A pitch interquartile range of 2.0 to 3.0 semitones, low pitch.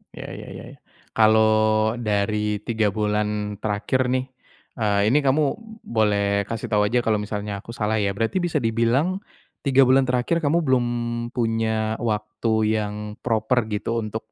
Yes: average, 2.7 semitones; low, 110 Hz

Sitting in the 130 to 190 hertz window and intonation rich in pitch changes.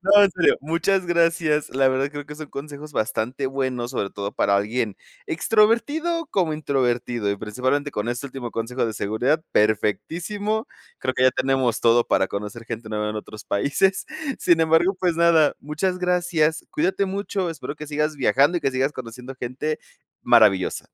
Yes: medium, 140 Hz; wide, 6.0 semitones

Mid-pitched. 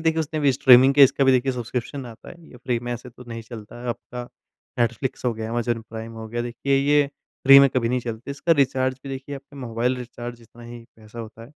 No: low, 125 Hz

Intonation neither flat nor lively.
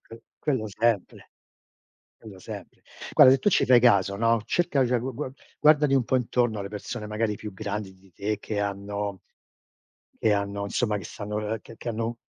Yes: average, 3.0 semitones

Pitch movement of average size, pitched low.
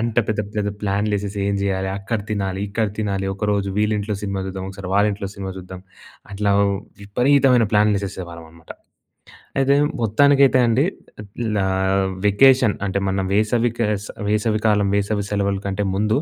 No: narrow, 1.9 semitones; low, 105 Hz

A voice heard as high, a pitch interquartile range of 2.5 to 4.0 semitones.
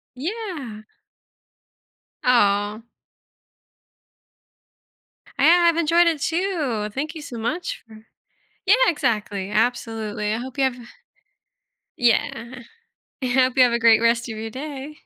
No: very high, 250 Hz; wide, 5.4 semitones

